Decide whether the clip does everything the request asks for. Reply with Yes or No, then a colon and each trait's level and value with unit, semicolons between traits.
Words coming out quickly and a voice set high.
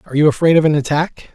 No: fast, 265 wpm; medium, 150 Hz